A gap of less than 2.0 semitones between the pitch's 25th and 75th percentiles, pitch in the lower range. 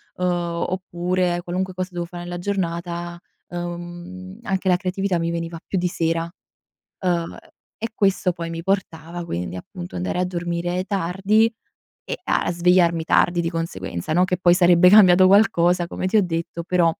No: narrow, 1.6 semitones; medium, 175 Hz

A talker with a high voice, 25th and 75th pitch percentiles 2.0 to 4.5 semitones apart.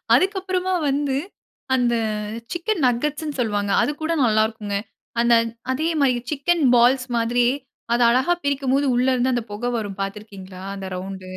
No: high, 245 Hz; average, 5.0 semitones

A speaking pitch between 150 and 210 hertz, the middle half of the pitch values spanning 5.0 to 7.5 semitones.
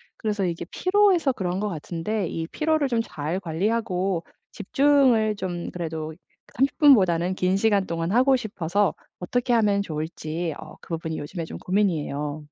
Yes: high, 190 Hz; wide, 5.5 semitones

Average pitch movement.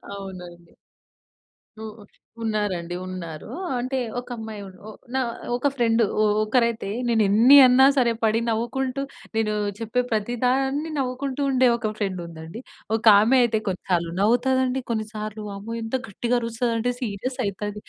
Yes: average, 3.5 semitones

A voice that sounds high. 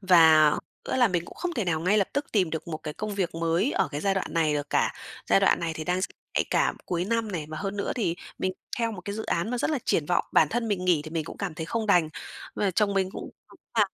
No: medium, 180 Hz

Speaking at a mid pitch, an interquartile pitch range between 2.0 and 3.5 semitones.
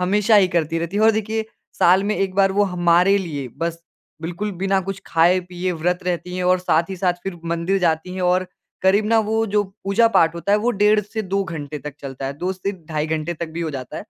Yes: medium, 180 Hz; average, 2.9 semitones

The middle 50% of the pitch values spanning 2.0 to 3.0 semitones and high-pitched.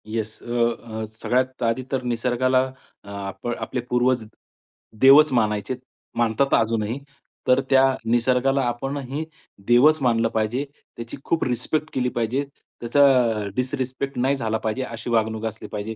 No: average, 2.7 semitones; low, 120 Hz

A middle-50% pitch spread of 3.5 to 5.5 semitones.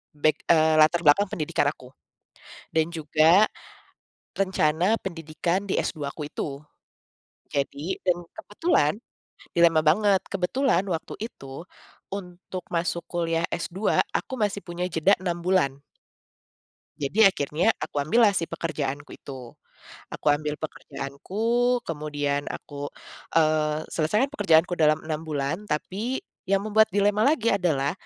Yes: average, 4.1 semitones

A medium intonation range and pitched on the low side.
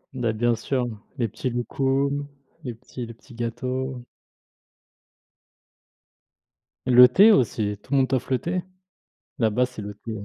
No: narrow, 2.3 semitones; low, 125 Hz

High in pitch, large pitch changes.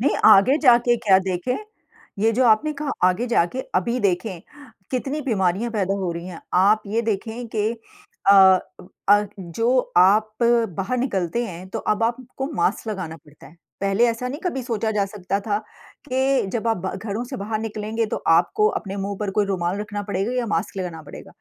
No: high, 210 Hz; average, 3.9 semitones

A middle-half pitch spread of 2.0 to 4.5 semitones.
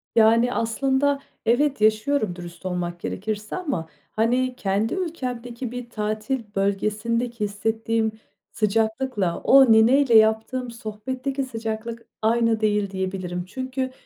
Yes: average, 3.3 semitones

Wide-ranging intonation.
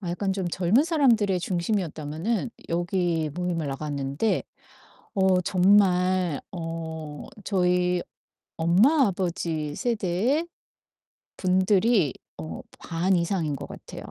No: average, 3.2 semitones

